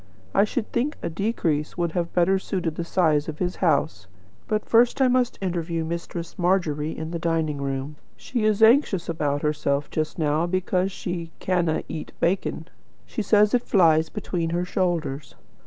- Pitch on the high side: No, medium, 170 Hz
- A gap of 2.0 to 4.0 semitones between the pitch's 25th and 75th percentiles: Yes, average, 3.6 semitones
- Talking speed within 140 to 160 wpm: No, average, 170 wpm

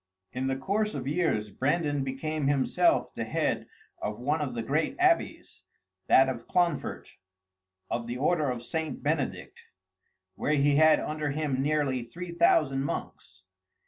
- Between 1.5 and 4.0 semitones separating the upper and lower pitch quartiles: Yes, average, 3.3 semitones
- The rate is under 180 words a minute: Yes, average, 145 wpm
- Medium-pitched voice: Yes, medium, 145 Hz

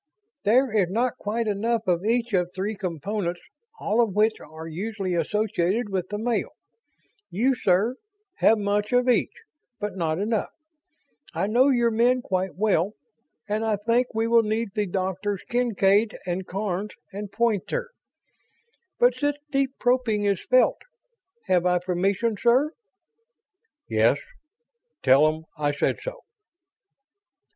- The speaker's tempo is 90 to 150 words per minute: Yes, slow, 135 wpm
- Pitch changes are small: No, average, 4.0 semitones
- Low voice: No, high, 210 Hz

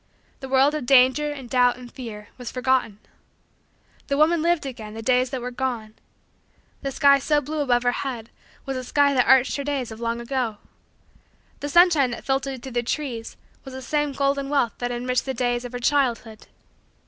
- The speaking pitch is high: Yes, very high, 260 Hz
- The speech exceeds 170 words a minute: Yes, average, 195 wpm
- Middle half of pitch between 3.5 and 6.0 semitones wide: No, narrow, 2.4 semitones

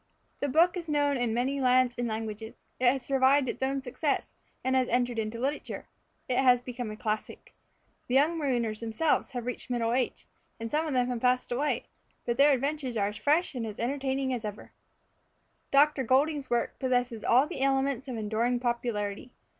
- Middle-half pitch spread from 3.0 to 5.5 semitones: No, narrow, 2.6 semitones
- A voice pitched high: Yes, very high, 250 Hz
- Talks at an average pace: Yes, average, 185 wpm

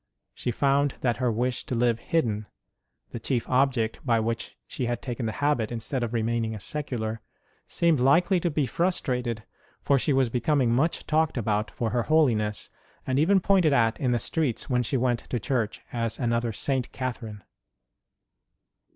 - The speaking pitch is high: No, low, 125 Hz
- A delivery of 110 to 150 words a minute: No, average, 175 wpm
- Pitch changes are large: No, average, 3.4 semitones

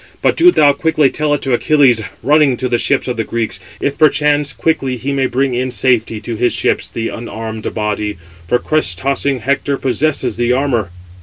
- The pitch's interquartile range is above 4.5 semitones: No, average, 3.4 semitones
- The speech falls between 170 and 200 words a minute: Yes, average, 190 wpm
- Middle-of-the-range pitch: No, low, 130 Hz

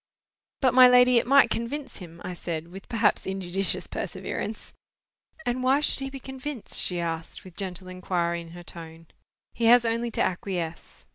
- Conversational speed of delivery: Yes, average, 170 wpm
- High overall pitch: Yes, high, 195 Hz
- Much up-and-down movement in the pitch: Yes, wide, 6.2 semitones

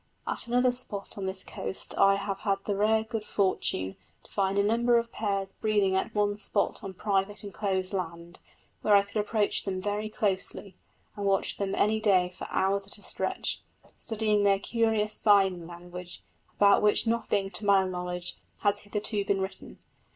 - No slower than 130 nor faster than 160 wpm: No, average, 175 wpm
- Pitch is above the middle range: Yes, high, 200 Hz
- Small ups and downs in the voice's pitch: Yes, narrow, 1.7 semitones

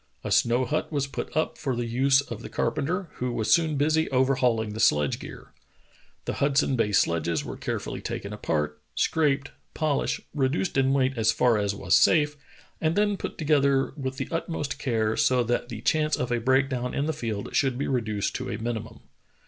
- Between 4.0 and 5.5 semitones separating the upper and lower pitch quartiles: Yes, average, 4.3 semitones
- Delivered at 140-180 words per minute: No, average, 200 wpm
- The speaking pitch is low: Yes, low, 130 Hz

